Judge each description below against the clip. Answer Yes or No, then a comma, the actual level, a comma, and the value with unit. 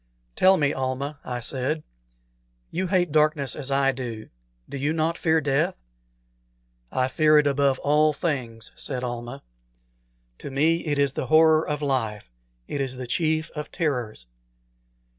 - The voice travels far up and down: No, average, 3.2 semitones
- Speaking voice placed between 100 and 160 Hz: Yes, medium, 140 Hz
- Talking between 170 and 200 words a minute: No, average, 150 wpm